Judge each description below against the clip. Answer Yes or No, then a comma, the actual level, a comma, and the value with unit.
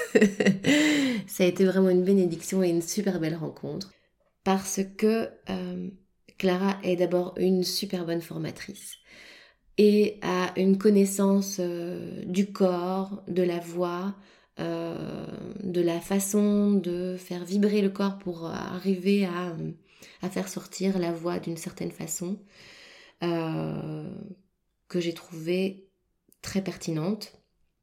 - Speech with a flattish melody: Yes, narrow, 1.9 semitones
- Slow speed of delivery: Yes, slow, 125 wpm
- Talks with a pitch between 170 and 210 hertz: Yes, medium, 185 Hz